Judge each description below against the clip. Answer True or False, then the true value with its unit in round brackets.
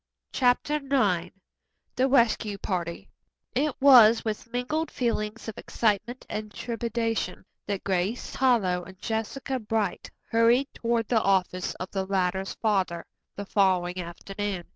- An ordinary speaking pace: False (125 wpm)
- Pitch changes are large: False (3.9 semitones)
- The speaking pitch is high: True (215 Hz)